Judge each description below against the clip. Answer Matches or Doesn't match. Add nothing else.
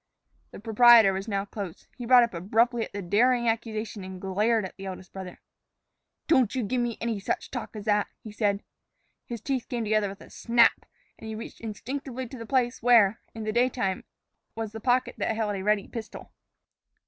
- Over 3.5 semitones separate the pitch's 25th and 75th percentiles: Doesn't match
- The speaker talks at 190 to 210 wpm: Matches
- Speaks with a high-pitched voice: Matches